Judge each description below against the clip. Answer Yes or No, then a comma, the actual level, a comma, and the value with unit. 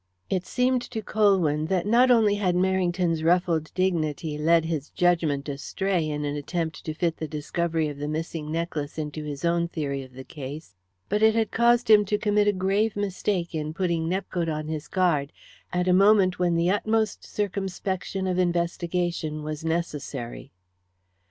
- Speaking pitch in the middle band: Yes, medium, 170 Hz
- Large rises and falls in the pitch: No, average, 3.8 semitones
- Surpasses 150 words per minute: Yes, average, 170 wpm